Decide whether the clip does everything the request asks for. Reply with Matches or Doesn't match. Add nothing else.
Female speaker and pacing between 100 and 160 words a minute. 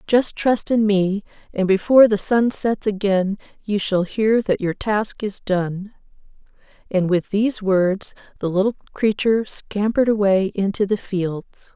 Matches